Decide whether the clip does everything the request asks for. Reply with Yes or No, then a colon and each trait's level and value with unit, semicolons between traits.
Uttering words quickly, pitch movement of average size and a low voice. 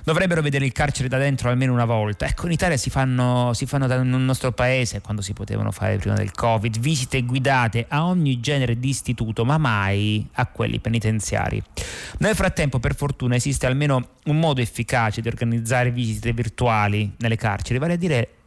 Yes: fast, 175 wpm; average, 3.2 semitones; low, 125 Hz